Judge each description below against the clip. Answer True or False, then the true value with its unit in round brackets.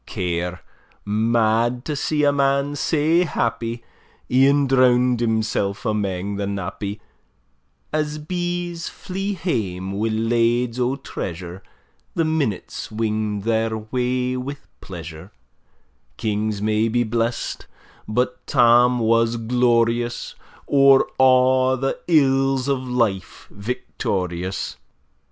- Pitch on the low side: True (120 Hz)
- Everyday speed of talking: False (105 wpm)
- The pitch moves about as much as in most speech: True (4.0 semitones)